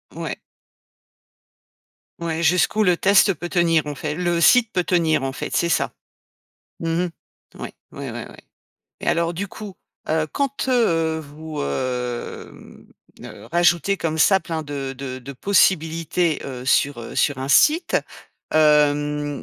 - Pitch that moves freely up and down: No, average, 3.4 semitones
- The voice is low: No, medium, 160 Hz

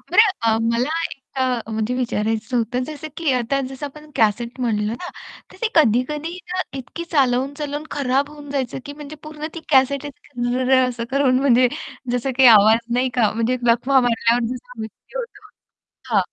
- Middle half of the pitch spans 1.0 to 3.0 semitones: No, average, 3.4 semitones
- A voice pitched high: Yes, very high, 255 Hz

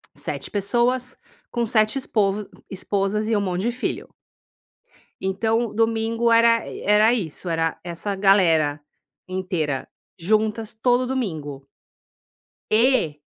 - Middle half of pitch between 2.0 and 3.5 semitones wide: No, average, 4.0 semitones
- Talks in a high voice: Yes, high, 210 Hz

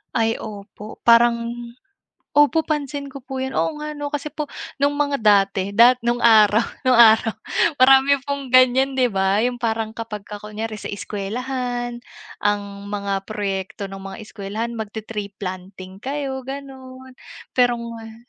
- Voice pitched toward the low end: No, high, 230 Hz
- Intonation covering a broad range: No, average, 4.2 semitones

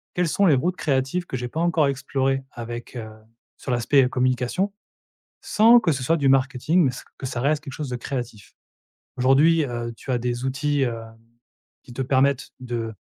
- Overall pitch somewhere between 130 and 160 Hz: Yes, low, 135 Hz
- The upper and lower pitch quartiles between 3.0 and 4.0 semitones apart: Yes, average, 3.3 semitones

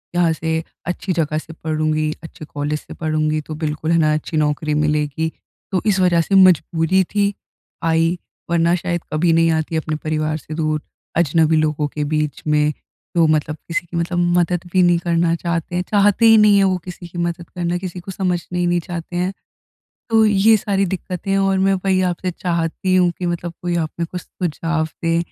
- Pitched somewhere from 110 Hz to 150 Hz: No, medium, 170 Hz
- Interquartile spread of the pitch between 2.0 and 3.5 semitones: Yes, narrow, 2.5 semitones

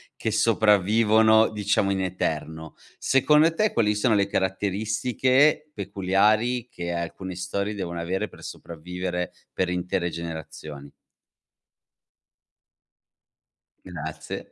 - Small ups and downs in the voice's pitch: No, average, 3.8 semitones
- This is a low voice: Yes, low, 100 Hz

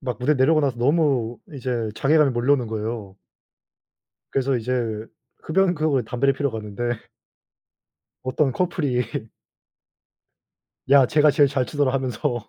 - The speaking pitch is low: Yes, low, 130 Hz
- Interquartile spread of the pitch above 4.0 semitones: No, average, 3.4 semitones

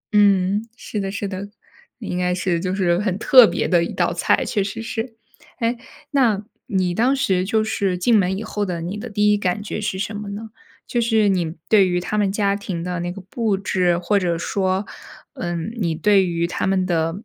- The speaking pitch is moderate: No, high, 195 Hz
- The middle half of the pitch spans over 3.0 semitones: No, average, 2.7 semitones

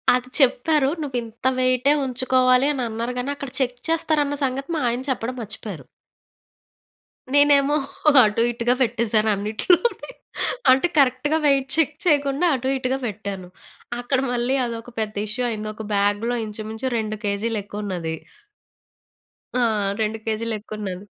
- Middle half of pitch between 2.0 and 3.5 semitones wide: No, average, 3.9 semitones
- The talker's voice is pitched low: No, high, 245 Hz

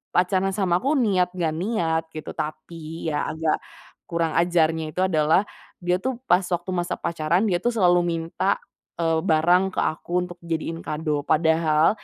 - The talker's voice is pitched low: No, medium, 170 Hz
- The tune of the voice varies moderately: No, narrow, 2.3 semitones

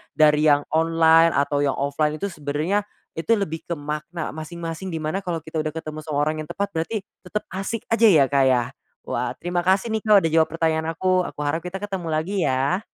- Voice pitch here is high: No, medium, 165 Hz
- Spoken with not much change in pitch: No, average, 3.5 semitones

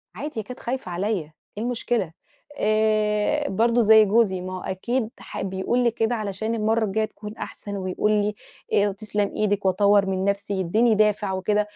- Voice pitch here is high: Yes, high, 210 Hz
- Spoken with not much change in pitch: Yes, narrow, 2.2 semitones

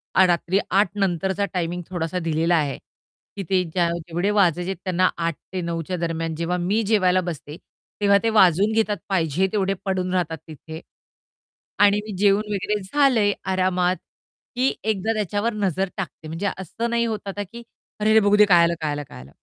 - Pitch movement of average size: Yes, average, 3.3 semitones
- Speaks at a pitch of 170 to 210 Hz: Yes, medium, 185 Hz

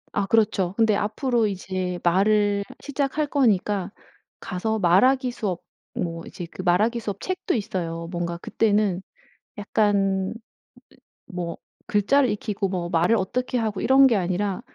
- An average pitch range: Yes, average, 3.7 semitones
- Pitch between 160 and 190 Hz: No, high, 205 Hz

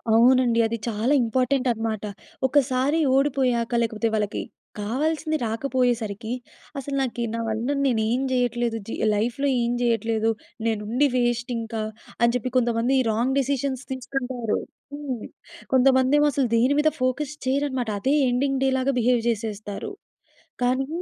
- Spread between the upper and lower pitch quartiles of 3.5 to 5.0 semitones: No, average, 2.7 semitones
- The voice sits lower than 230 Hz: No, high, 245 Hz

